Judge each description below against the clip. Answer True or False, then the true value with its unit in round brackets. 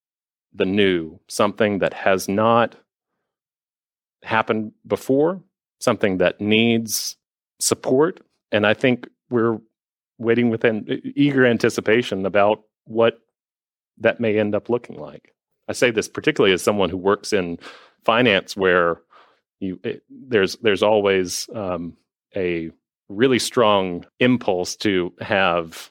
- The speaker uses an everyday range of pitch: True (3.5 semitones)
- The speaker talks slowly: True (120 wpm)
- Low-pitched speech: True (105 Hz)